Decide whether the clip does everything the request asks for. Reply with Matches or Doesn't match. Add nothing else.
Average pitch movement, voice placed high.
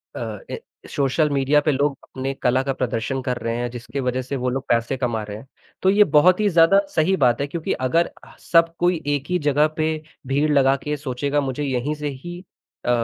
Doesn't match